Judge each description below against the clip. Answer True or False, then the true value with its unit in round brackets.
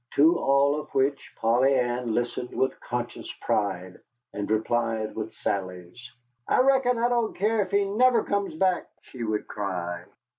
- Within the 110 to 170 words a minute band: True (155 wpm)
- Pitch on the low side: True (125 Hz)